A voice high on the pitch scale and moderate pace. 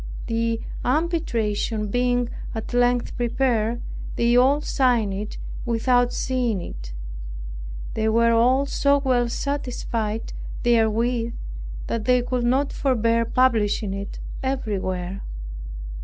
No: high, 235 Hz; slow, 105 wpm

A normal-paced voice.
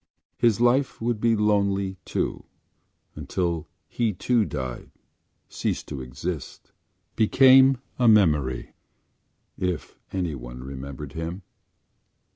No: slow, 90 wpm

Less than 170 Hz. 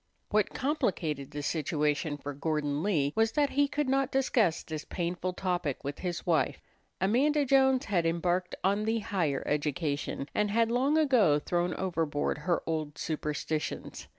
No: medium, 175 Hz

